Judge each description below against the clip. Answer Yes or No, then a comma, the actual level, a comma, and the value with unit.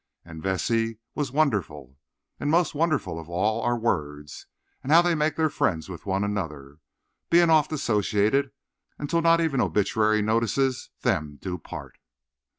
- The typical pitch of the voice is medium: No, low, 110 Hz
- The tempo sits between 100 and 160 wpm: Yes, average, 145 wpm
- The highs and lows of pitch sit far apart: Yes, wide, 8.6 semitones